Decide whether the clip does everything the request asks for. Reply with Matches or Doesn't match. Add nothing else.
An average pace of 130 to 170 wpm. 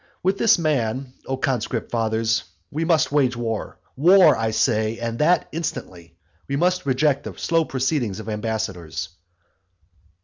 Matches